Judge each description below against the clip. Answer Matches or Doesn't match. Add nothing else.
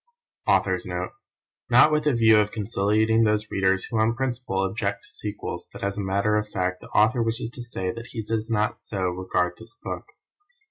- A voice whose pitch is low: Matches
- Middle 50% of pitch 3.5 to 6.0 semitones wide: Doesn't match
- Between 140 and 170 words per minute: Doesn't match